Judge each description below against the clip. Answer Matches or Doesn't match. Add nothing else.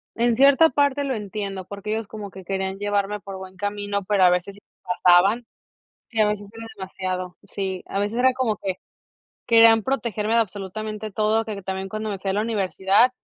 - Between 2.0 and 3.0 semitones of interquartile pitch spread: Matches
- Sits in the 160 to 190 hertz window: Doesn't match